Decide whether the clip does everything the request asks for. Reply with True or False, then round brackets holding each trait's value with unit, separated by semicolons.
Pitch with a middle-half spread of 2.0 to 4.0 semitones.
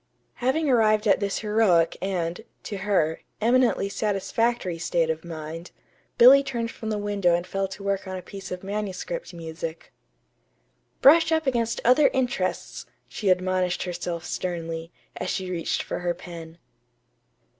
False (4.7 semitones)